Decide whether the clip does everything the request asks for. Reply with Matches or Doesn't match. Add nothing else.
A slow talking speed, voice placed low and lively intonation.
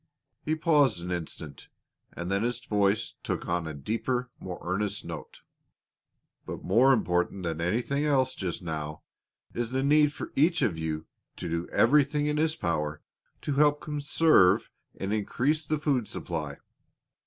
Doesn't match